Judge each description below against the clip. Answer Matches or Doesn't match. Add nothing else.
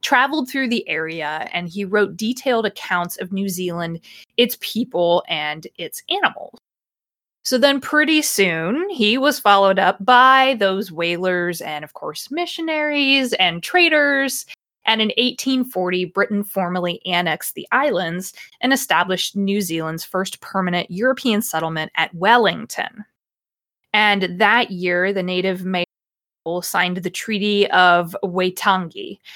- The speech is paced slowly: Matches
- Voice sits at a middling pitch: Doesn't match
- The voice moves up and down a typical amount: Doesn't match